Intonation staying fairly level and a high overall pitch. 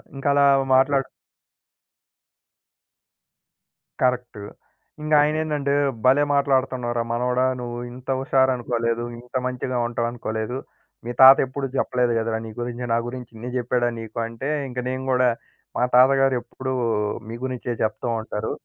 No: narrow, 1.9 semitones; low, 125 Hz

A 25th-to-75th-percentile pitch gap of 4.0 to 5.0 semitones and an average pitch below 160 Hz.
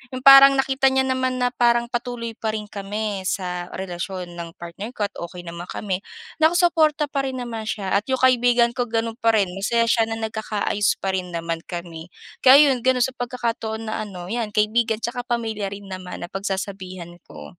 No: average, 4.4 semitones; high, 220 Hz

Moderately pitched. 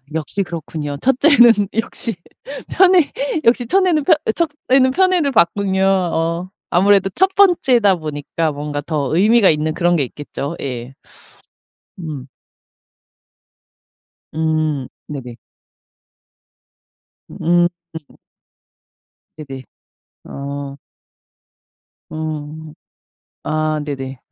Yes: medium, 165 Hz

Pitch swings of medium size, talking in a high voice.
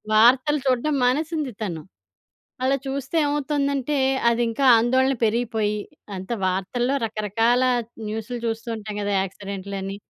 Yes: average, 4.3 semitones; high, 235 Hz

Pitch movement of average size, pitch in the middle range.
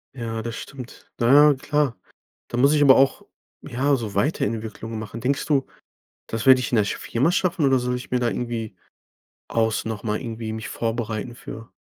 No: average, 3.0 semitones; low, 120 Hz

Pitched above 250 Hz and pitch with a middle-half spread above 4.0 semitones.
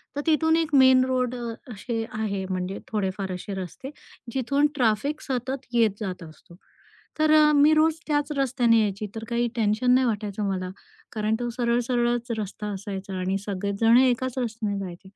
No: high, 230 Hz; average, 4.4 semitones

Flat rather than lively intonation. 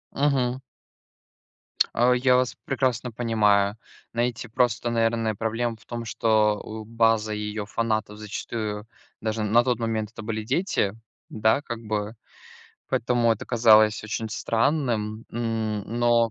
Yes: narrow, 1.8 semitones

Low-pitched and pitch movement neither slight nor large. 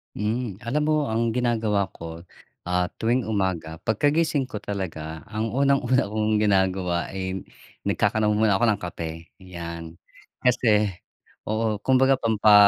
Yes: low, 105 Hz; average, 4.5 semitones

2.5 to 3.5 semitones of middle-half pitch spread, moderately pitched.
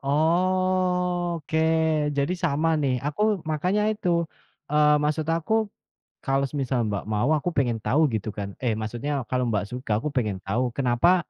No: average, 5.3 semitones; medium, 150 Hz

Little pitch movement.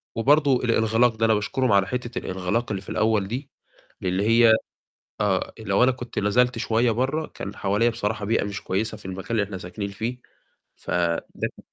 No: average, 3.2 semitones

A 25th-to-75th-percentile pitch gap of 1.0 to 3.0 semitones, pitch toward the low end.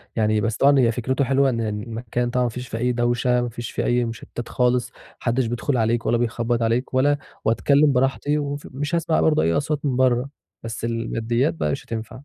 Yes: narrow, 2.5 semitones; low, 120 Hz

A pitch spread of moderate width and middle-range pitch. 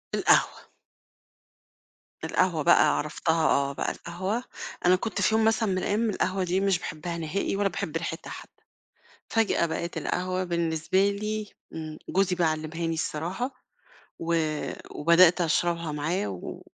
Yes: average, 3.3 semitones; medium, 175 Hz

